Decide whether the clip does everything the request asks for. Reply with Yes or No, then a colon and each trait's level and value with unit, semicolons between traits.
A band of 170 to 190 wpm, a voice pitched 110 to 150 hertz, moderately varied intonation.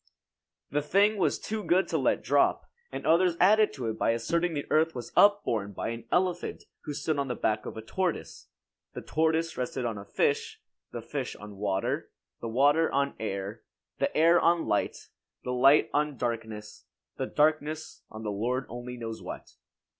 No: average, 180 wpm; medium, 140 Hz; wide, 6.5 semitones